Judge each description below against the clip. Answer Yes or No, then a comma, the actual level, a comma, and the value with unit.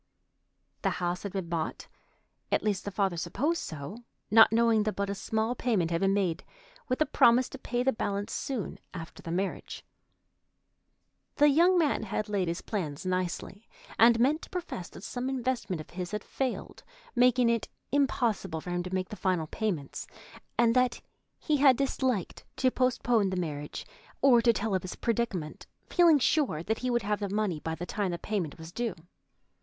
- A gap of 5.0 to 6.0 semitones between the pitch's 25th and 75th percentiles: Yes, wide, 5.4 semitones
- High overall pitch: Yes, high, 210 Hz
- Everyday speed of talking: Yes, average, 180 wpm